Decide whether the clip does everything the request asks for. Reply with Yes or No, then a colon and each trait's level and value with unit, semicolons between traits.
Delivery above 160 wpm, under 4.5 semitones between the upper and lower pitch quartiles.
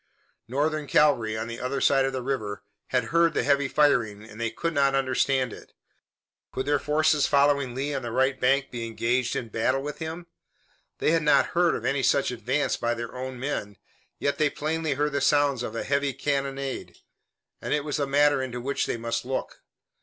Yes: average, 200 wpm; average, 2.9 semitones